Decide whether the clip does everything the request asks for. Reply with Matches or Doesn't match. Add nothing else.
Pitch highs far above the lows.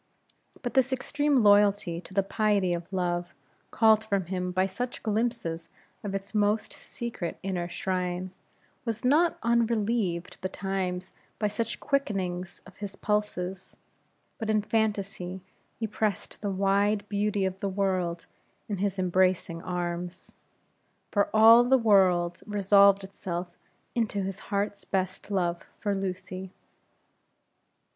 Doesn't match